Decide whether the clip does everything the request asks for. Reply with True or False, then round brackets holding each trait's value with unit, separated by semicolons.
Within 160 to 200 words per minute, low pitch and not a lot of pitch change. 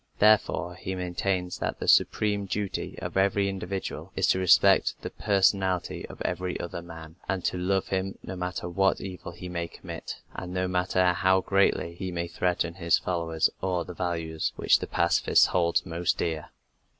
True (175 wpm; 90 Hz; 1.7 semitones)